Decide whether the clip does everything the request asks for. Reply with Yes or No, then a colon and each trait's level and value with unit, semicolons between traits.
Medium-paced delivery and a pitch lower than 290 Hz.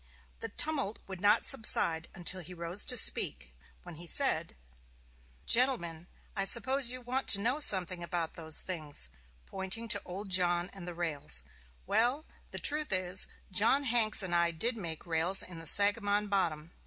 Yes: average, 165 wpm; high, 190 Hz